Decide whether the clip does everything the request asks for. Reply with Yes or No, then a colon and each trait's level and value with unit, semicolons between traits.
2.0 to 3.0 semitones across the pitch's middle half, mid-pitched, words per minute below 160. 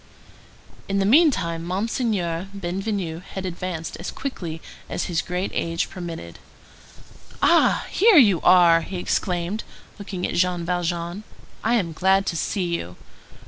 Yes: average, 2.7 semitones; medium, 180 Hz; slow, 135 wpm